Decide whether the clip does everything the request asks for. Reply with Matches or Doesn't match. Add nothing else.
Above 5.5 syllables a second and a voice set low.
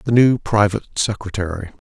Matches